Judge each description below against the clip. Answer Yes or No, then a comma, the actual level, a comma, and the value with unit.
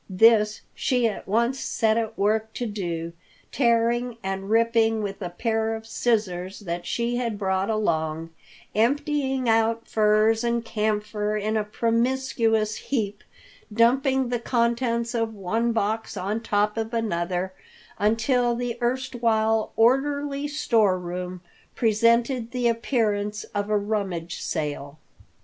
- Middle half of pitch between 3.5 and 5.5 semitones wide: No, narrow, 2.4 semitones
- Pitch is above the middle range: Yes, high, 225 Hz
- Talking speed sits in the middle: No, slow, 125 wpm